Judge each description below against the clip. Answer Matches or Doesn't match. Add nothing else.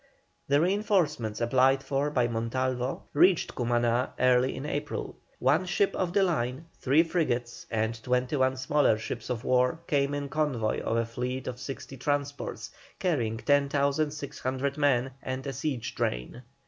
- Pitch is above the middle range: Doesn't match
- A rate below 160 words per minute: Matches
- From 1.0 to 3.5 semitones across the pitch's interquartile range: Matches